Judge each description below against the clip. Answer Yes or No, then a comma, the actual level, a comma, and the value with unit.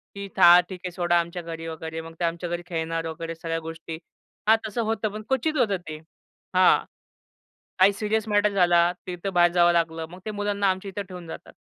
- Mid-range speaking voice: Yes, medium, 175 Hz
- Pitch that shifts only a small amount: No, average, 3.4 semitones